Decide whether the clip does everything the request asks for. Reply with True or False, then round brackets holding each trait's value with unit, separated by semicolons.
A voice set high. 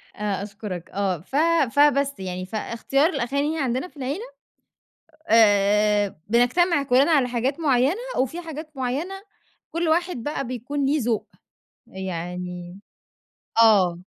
True (245 Hz)